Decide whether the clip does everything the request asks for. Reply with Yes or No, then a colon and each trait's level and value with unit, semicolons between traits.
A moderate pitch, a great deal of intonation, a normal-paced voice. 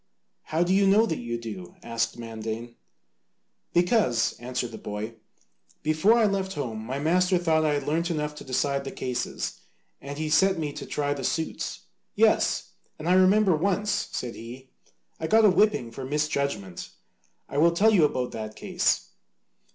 Yes: medium, 150 Hz; wide, 7.1 semitones; average, 170 wpm